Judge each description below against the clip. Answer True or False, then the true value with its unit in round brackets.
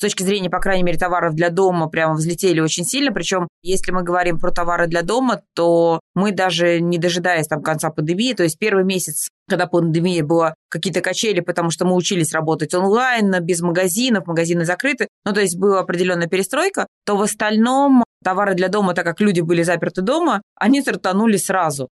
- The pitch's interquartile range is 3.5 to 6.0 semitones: False (2.8 semitones)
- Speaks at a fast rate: True (190 wpm)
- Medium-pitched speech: True (180 Hz)